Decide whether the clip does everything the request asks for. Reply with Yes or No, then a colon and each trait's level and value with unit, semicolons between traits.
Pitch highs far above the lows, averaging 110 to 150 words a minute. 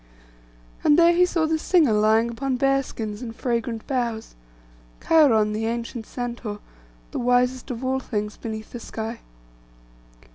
No: average, 3.4 semitones; average, 145 wpm